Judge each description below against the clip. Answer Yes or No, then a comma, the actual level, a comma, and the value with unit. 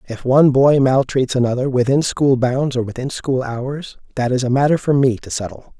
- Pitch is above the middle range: No, low, 130 Hz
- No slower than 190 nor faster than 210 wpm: Yes, fast, 205 wpm